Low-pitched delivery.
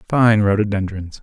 Yes: low, 105 Hz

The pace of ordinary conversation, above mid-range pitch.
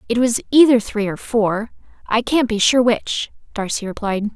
Yes: average, 180 wpm; high, 225 Hz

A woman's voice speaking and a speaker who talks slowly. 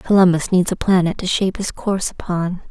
No: female; average, 200 wpm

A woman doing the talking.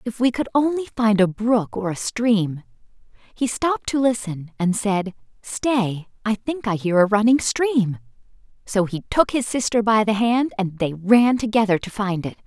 Yes: female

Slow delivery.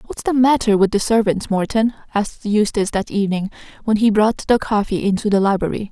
No: average, 195 wpm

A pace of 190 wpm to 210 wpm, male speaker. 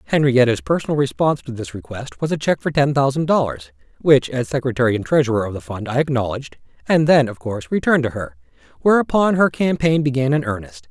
Yes: average, 200 wpm; male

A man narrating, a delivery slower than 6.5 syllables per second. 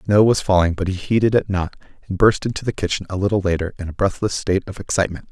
No: male; 6.9 syllables/s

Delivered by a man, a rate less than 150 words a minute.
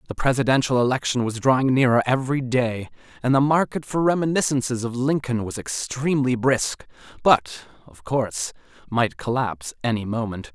Yes: male; average, 140 wpm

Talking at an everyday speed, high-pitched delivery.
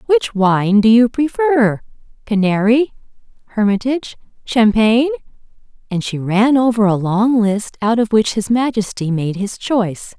No: slow, 130 wpm; high, 225 Hz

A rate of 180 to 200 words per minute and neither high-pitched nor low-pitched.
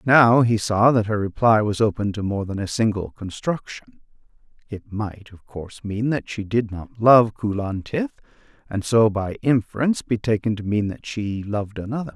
No: average, 190 wpm; low, 110 Hz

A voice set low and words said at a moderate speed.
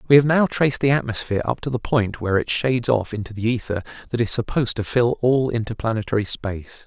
No: low, 115 Hz; fast, 220 wpm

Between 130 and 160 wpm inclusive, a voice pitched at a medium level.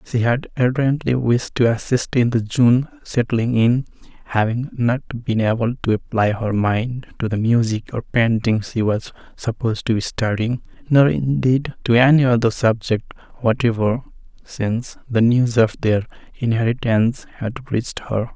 No: average, 150 wpm; low, 120 Hz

